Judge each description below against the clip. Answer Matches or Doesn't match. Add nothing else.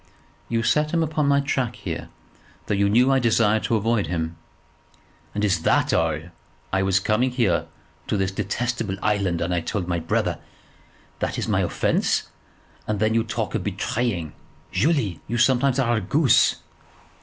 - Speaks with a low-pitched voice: Matches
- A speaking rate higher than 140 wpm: Matches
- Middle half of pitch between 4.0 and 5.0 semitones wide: Matches